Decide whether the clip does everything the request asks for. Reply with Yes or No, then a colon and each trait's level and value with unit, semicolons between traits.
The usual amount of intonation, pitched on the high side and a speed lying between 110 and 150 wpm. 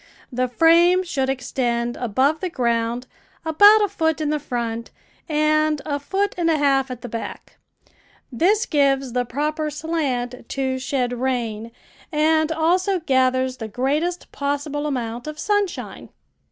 Yes: average, 4.4 semitones; very high, 280 Hz; average, 140 wpm